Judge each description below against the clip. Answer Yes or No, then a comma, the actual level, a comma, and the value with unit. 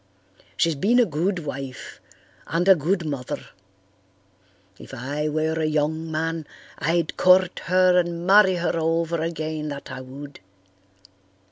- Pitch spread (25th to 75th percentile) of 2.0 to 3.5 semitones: Yes, average, 2.7 semitones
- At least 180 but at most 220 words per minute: No, slow, 135 wpm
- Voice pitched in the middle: Yes, medium, 160 Hz